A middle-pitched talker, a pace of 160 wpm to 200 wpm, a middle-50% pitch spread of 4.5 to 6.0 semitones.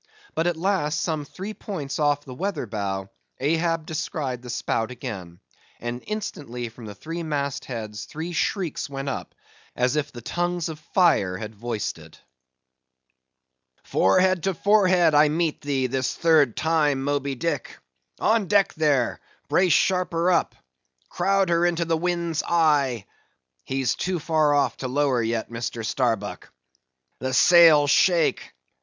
No: medium, 150 Hz; average, 145 wpm; average, 5.3 semitones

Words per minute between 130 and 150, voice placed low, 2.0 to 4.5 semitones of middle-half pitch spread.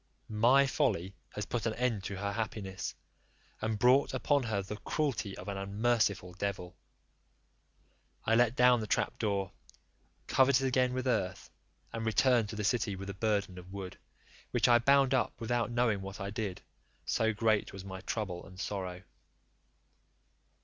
No: average, 165 wpm; low, 110 Hz; average, 3.8 semitones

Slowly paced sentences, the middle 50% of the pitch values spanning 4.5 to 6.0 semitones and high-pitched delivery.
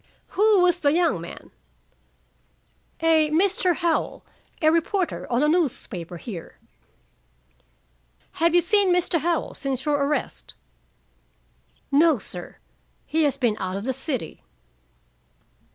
Yes: slow, 120 wpm; average, 5.2 semitones; very high, 310 Hz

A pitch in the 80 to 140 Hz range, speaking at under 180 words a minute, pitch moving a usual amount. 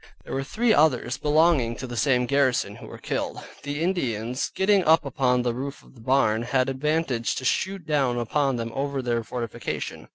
No: low, 135 Hz; average, 190 wpm; average, 3.7 semitones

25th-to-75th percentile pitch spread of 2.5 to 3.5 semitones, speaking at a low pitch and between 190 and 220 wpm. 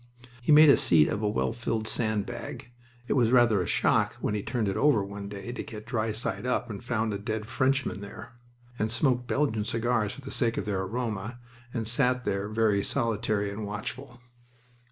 Yes: average, 2.9 semitones; low, 110 Hz; average, 200 wpm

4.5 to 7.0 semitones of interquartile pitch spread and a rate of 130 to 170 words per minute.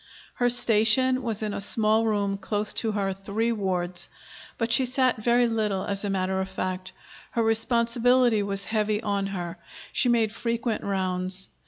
No: average, 3.1 semitones; average, 165 wpm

